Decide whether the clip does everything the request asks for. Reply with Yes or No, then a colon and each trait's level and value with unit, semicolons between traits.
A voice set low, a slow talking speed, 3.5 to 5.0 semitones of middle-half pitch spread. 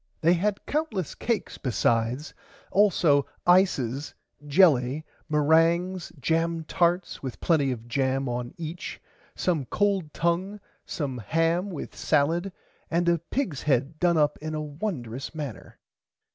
No: medium, 160 Hz; slow, 125 wpm; average, 4.2 semitones